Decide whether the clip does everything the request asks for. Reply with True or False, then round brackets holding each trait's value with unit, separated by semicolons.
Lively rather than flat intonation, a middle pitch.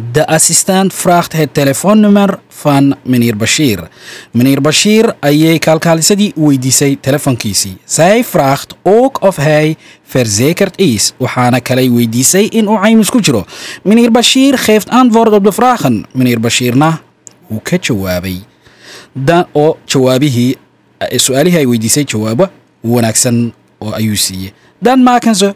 True (8.2 semitones; 150 Hz)